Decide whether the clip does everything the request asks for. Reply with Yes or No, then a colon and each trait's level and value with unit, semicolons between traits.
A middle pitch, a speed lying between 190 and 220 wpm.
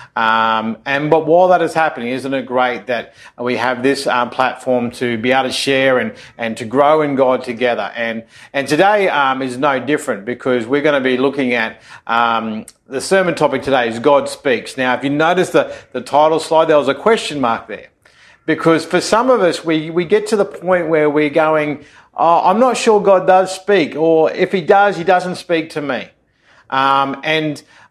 Yes: medium, 145 Hz; fast, 205 wpm